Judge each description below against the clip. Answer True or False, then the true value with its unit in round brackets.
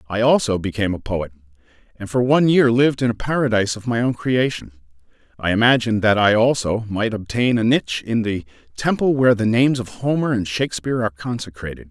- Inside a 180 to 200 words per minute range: True (190 wpm)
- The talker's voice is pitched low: True (115 Hz)